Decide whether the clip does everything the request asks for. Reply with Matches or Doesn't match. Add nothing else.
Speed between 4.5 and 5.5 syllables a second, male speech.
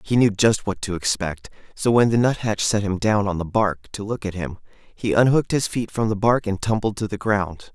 Matches